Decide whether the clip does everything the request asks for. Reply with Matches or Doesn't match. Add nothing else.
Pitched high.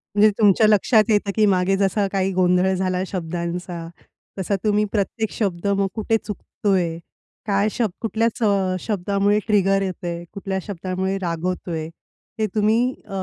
Matches